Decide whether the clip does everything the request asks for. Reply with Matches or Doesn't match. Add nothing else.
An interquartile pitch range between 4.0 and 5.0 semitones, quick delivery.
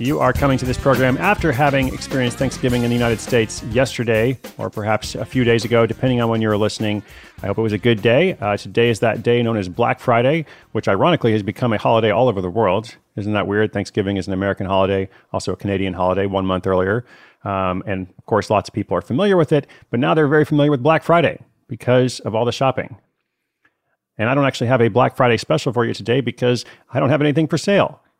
Matches